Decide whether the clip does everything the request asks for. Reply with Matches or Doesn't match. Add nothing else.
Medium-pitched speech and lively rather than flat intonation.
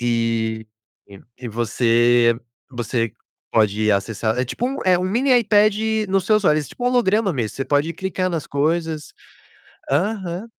Matches